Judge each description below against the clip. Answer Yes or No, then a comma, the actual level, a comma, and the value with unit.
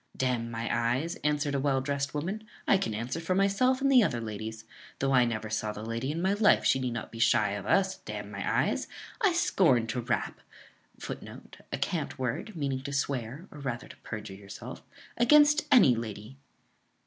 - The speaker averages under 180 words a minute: No, average, 200 wpm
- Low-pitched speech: Yes, low, 130 Hz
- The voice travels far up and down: Yes, wide, 7.3 semitones